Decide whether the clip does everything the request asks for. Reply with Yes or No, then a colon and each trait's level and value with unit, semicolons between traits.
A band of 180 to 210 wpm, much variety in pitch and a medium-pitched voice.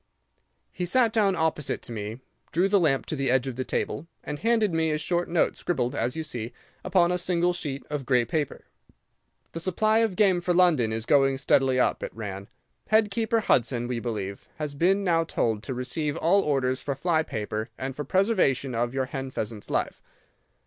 Yes: average, 195 wpm; wide, 6.0 semitones; medium, 150 Hz